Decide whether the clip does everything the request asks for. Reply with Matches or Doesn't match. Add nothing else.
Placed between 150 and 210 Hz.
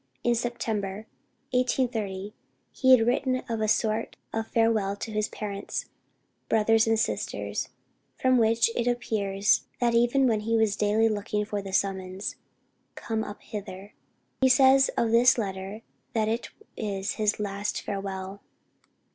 Doesn't match